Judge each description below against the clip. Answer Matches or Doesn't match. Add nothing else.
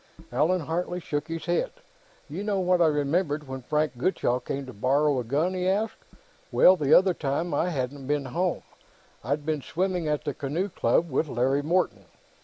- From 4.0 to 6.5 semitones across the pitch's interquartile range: Matches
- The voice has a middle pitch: Matches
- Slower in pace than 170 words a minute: Doesn't match